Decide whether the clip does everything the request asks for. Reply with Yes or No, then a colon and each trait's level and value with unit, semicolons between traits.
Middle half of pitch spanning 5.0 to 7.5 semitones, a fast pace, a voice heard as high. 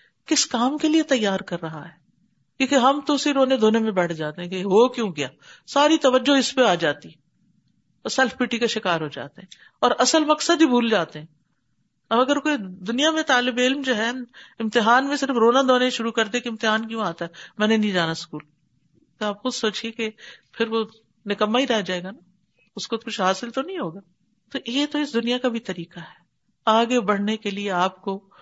Yes: average, 5.3 semitones; fast, 220 wpm; high, 225 Hz